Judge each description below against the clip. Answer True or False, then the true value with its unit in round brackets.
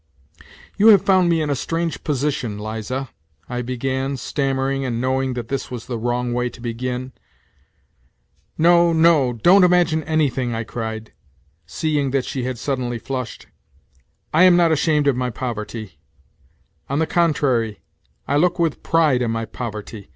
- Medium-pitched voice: False (130 Hz)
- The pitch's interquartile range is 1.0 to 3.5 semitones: False (4.7 semitones)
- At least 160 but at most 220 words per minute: True (165 wpm)